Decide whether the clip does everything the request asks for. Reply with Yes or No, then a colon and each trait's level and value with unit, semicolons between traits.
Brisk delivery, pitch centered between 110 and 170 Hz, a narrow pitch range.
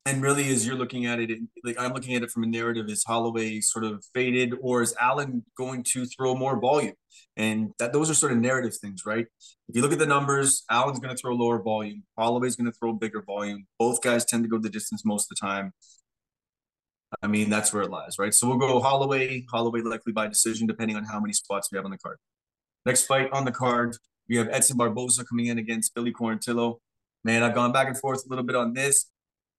Yes: fast, 235 wpm; low, 120 Hz; narrow, 2.3 semitones